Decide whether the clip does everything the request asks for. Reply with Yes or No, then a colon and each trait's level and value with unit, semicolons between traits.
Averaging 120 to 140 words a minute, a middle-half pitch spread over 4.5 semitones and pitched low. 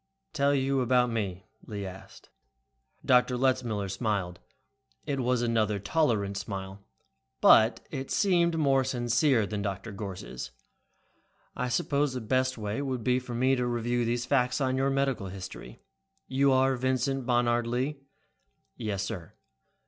No: slow, 135 wpm; average, 4.1 semitones; low, 120 Hz